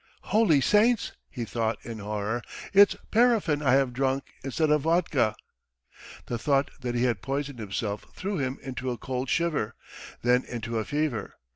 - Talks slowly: No, average, 160 wpm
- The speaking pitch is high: No, low, 130 Hz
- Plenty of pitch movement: No, average, 4.5 semitones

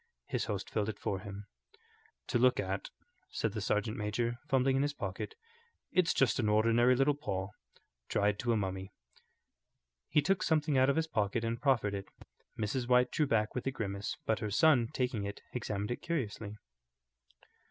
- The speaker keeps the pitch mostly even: No, average, 4.4 semitones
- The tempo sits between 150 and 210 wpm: Yes, average, 175 wpm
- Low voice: Yes, low, 115 Hz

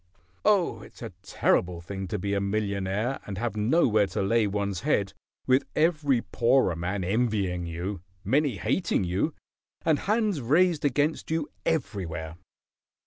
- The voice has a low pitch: Yes, low, 105 Hz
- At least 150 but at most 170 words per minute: No, average, 140 wpm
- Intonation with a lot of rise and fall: Yes, wide, 7.0 semitones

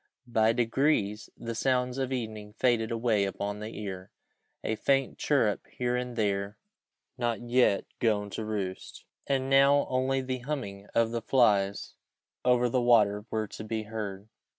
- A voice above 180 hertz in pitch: No, low, 115 Hz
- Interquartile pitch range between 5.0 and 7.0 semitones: No, average, 3.3 semitones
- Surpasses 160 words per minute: Yes, average, 170 wpm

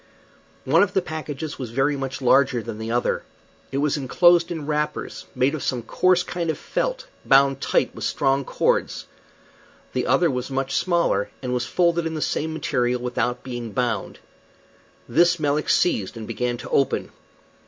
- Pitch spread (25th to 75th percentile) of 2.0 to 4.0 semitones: No, average, 4.6 semitones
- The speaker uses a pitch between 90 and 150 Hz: Yes, medium, 140 Hz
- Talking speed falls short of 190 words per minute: Yes, average, 170 wpm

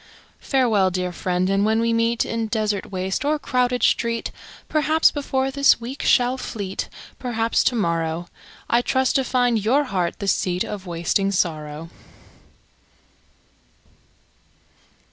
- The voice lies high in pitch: Yes, high, 225 Hz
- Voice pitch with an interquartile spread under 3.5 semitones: No, average, 5.2 semitones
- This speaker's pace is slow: Yes, slow, 130 wpm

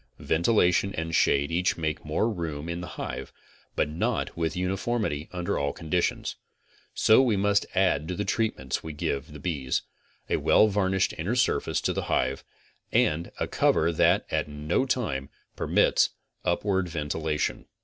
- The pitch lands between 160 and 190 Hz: No, very low, 85 Hz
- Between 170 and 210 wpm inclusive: No, average, 160 wpm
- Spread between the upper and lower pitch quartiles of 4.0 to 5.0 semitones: Yes, average, 4.3 semitones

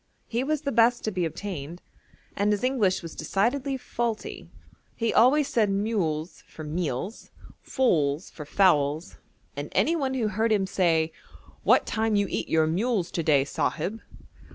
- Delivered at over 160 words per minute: No, average, 155 wpm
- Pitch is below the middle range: No, high, 200 Hz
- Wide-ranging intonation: Yes, wide, 6.4 semitones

